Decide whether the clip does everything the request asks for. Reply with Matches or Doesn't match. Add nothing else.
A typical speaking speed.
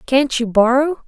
Matches